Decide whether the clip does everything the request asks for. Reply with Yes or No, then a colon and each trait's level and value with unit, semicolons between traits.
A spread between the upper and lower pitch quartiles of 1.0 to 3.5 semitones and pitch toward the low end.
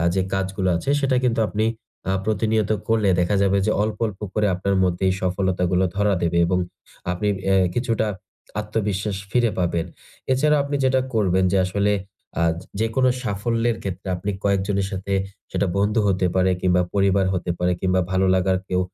Yes: average, 2.7 semitones; low, 100 Hz